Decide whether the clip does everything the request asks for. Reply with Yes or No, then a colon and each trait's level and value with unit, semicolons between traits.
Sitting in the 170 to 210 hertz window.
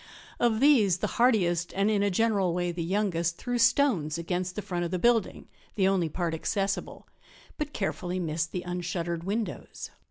Yes: medium, 185 Hz